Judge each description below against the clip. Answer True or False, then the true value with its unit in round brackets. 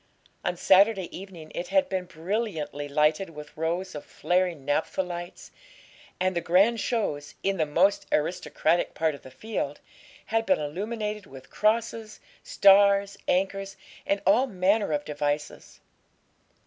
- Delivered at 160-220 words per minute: False (135 wpm)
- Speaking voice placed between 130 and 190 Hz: True (185 Hz)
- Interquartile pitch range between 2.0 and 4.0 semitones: False (4.6 semitones)